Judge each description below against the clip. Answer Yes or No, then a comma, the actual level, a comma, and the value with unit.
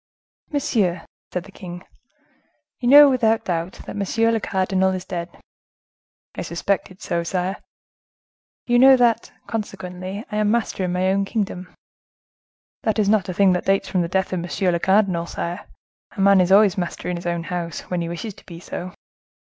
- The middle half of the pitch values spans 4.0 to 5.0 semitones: No, average, 3.0 semitones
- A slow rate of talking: No, average, 180 wpm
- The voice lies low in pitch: No, high, 190 Hz